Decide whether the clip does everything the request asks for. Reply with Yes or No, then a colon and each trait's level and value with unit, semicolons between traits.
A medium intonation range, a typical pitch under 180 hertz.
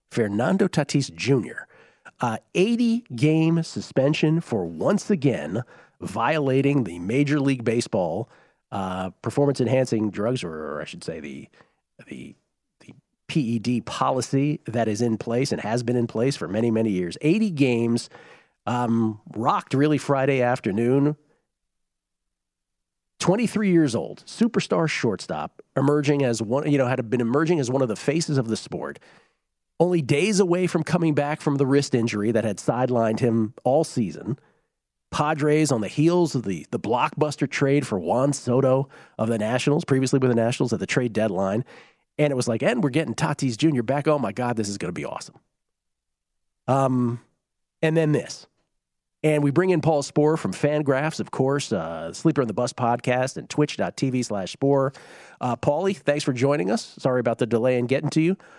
Yes: average, 4.4 semitones; low, 135 Hz